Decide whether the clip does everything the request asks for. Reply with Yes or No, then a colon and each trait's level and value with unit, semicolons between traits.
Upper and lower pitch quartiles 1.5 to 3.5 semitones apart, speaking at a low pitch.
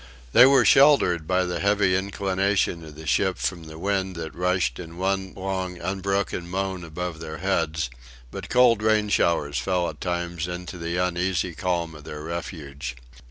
Yes: narrow, 2.6 semitones; very low, 90 Hz